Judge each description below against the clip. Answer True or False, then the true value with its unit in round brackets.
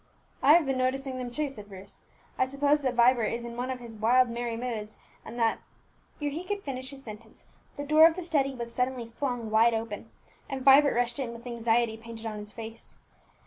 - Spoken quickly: True (220 wpm)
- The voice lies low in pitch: False (245 Hz)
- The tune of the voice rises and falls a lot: False (3.0 semitones)